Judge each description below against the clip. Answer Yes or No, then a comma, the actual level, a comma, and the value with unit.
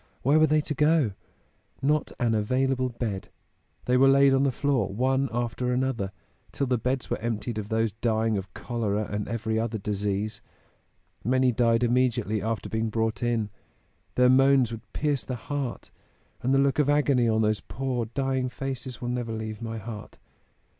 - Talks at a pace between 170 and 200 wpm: Yes, average, 175 wpm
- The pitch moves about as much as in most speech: Yes, average, 3.2 semitones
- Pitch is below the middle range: Yes, low, 120 Hz